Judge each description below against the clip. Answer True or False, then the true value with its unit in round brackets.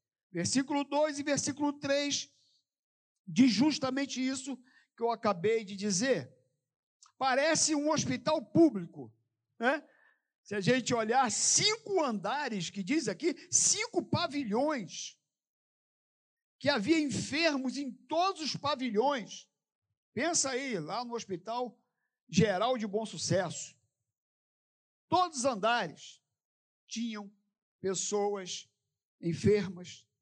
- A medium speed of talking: False (100 wpm)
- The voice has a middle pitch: False (240 Hz)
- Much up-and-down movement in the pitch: True (6.9 semitones)